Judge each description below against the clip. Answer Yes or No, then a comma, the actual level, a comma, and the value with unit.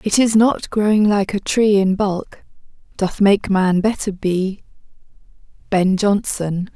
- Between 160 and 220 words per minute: No, average, 140 wpm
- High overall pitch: Yes, high, 200 Hz